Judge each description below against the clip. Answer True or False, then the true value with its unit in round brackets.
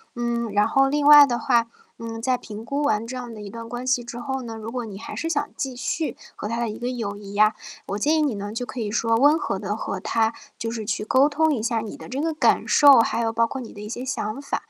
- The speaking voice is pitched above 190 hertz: True (235 Hz)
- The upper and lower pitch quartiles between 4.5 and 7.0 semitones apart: False (3.3 semitones)